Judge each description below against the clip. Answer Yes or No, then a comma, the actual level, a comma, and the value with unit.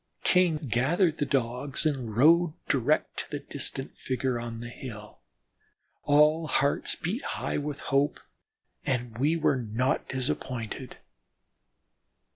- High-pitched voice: No, low, 135 Hz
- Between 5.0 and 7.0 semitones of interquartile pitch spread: No, average, 3.7 semitones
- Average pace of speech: No, slow, 120 wpm